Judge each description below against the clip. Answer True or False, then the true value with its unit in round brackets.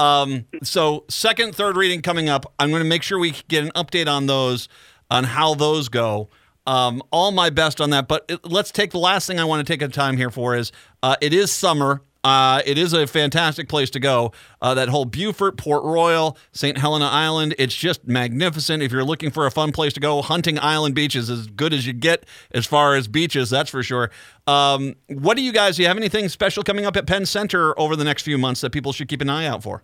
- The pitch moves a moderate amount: True (3.8 semitones)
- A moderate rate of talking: False (245 wpm)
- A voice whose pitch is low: False (150 Hz)